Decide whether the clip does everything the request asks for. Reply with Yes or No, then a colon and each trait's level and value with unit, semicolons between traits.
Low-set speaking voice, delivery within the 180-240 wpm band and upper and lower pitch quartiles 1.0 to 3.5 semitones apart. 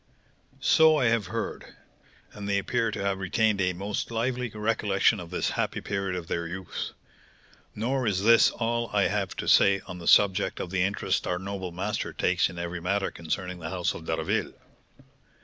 Yes: low, 100 Hz; average, 185 wpm; average, 2.9 semitones